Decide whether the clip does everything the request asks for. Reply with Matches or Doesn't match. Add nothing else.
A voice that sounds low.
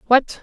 Doesn't match